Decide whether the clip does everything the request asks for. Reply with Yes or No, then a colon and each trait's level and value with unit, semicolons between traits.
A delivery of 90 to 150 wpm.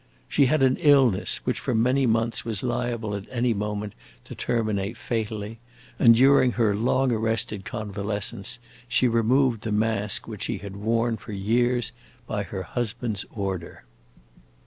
Yes: average, 145 wpm